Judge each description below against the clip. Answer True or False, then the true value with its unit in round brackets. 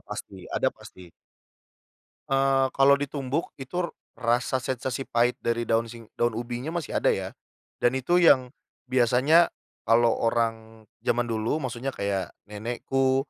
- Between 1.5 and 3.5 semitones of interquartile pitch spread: True (2.7 semitones)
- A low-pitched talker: True (125 Hz)